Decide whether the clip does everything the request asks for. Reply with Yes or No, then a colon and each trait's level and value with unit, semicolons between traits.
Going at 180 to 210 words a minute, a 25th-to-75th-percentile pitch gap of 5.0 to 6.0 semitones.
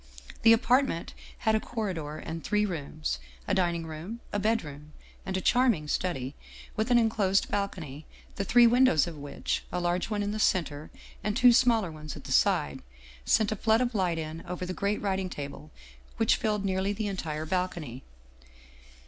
Yes: average, 185 wpm; wide, 5.5 semitones